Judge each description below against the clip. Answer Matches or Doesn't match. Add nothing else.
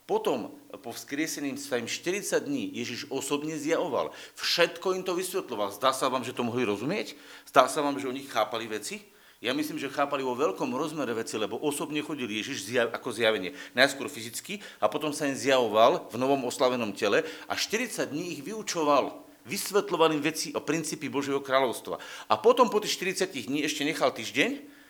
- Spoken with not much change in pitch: Doesn't match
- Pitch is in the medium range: Matches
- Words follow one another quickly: Matches